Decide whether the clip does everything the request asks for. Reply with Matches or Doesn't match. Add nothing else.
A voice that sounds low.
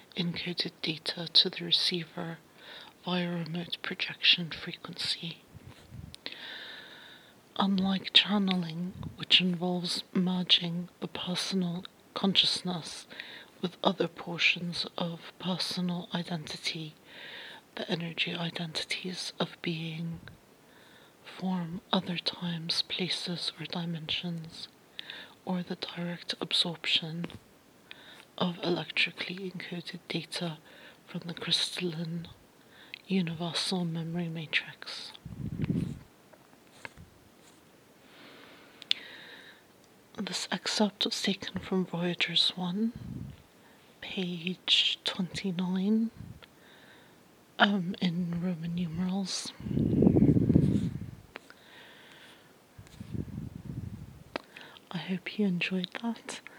Doesn't match